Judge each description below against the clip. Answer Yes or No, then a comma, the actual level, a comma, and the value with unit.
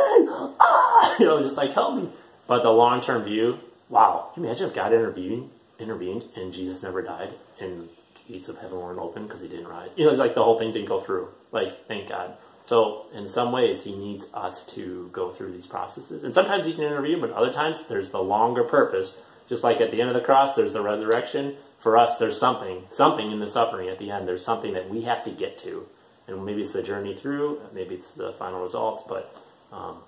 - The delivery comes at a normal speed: No, fast, 225 wpm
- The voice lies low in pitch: Yes, low, 115 Hz